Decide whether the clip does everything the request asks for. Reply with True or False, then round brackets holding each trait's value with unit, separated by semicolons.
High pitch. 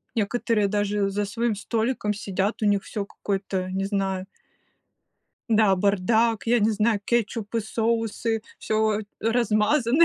True (215 Hz)